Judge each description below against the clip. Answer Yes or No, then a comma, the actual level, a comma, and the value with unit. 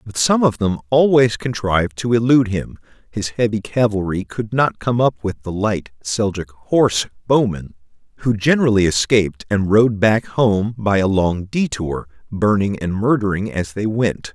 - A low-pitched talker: Yes, low, 110 Hz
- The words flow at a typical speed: Yes, average, 165 wpm